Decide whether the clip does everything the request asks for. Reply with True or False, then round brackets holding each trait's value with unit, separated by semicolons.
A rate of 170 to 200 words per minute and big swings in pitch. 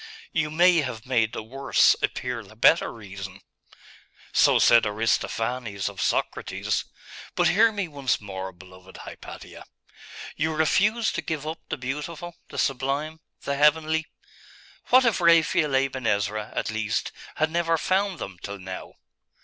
False (140 wpm; 7.0 semitones)